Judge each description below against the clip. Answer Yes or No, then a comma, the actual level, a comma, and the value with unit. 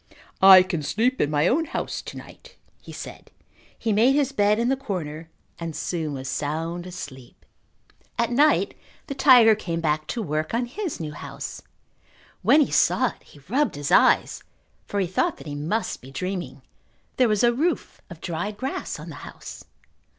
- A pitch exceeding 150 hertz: Yes, high, 190 Hz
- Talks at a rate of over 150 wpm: Yes, average, 180 wpm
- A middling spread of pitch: No, wide, 7.6 semitones